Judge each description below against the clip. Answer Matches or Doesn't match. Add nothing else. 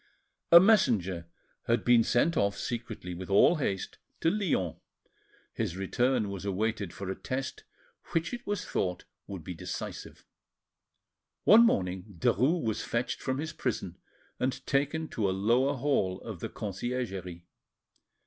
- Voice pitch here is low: Matches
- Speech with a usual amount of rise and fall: Doesn't match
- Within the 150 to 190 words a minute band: Doesn't match